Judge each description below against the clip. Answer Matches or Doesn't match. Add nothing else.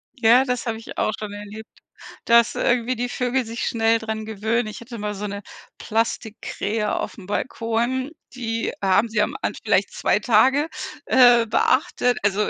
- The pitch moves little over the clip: Matches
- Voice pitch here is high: Matches